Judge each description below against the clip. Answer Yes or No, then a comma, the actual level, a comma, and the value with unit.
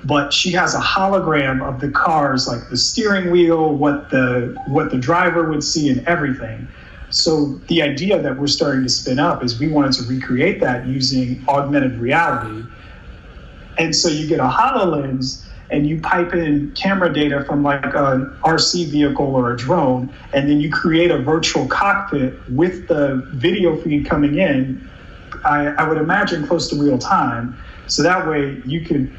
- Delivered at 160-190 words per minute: Yes, average, 175 wpm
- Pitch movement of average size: Yes, average, 3.8 semitones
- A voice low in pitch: No, medium, 145 Hz